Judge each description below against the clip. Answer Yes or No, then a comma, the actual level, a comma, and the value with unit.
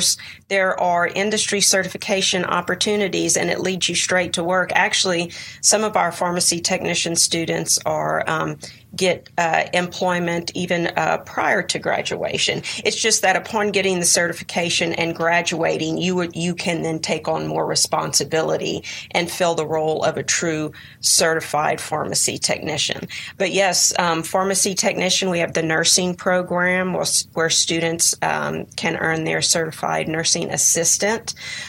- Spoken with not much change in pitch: Yes, narrow, 2.3 semitones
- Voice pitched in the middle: Yes, medium, 175 Hz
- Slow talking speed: No, average, 145 wpm